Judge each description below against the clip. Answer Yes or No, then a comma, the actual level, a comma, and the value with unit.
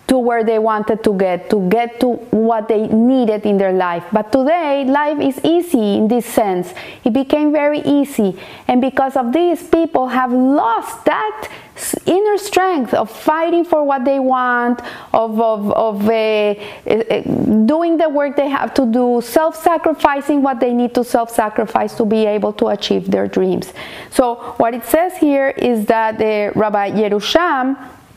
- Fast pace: No, average, 170 wpm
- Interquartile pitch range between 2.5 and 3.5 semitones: No, average, 4.7 semitones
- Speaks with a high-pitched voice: Yes, very high, 250 Hz